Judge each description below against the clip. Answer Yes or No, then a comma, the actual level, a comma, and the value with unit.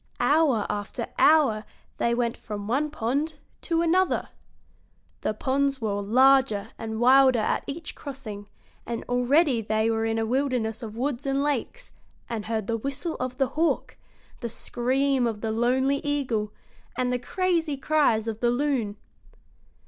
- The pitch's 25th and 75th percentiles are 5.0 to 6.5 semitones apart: No, average, 4.0 semitones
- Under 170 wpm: Yes, average, 150 wpm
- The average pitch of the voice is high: Yes, very high, 250 Hz